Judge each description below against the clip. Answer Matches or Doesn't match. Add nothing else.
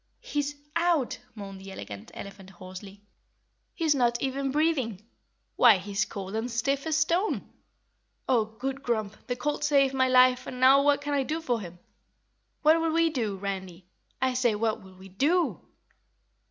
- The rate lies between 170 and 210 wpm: Doesn't match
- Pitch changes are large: Matches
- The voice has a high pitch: Matches